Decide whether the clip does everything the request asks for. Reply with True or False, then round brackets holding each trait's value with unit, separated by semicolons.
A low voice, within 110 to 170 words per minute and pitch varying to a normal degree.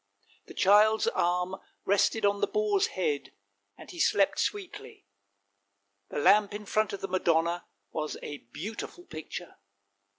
False (200 Hz; 135 wpm; 4.4 semitones)